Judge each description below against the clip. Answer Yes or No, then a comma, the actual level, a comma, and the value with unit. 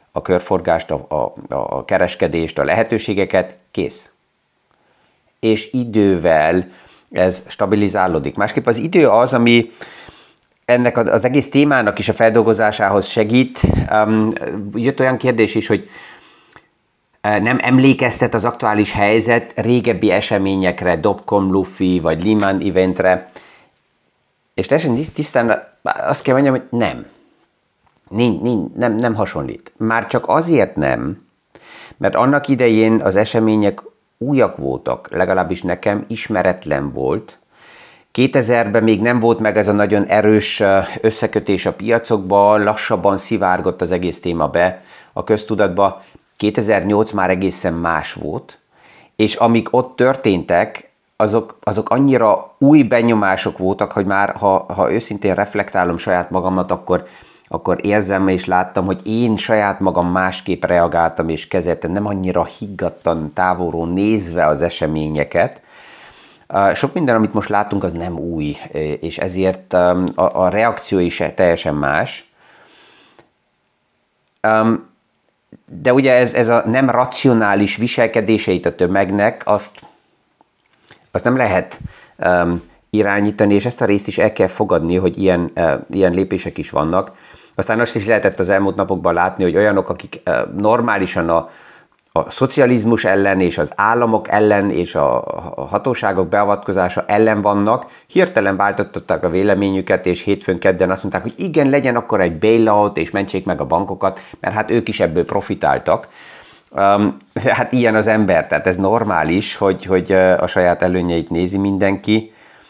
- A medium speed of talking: Yes, average, 130 wpm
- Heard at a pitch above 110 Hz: No, low, 100 Hz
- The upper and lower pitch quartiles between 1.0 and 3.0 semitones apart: No, average, 3.4 semitones